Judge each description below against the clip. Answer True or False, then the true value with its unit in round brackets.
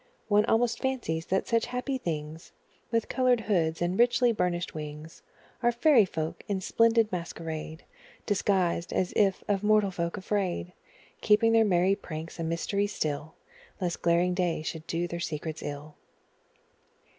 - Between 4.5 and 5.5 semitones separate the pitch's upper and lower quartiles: True (5.0 semitones)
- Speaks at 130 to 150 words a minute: True (145 wpm)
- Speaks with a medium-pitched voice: True (180 Hz)